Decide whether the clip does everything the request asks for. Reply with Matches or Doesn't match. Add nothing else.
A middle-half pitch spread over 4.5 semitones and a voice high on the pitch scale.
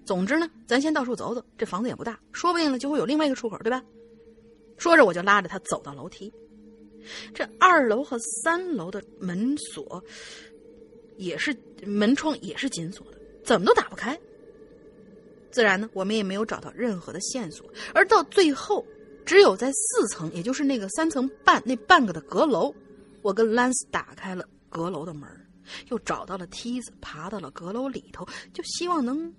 Matches